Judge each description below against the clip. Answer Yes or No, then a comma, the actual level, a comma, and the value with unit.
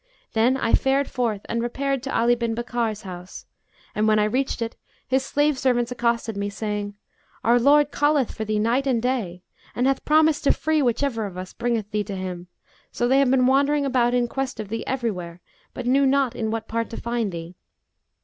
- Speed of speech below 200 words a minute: No, fast, 205 wpm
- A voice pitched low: No, high, 240 Hz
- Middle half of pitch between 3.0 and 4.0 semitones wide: Yes, average, 3.7 semitones